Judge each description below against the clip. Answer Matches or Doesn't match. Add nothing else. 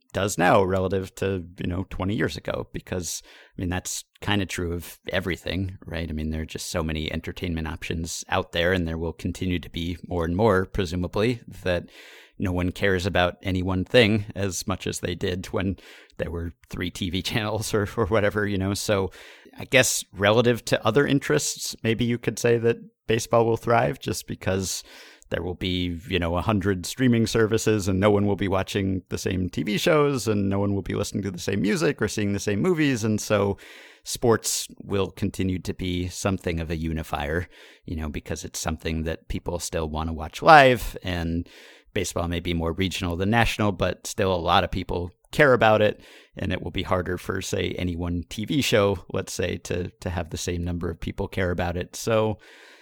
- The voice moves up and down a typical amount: Matches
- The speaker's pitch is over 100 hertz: Doesn't match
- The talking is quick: Matches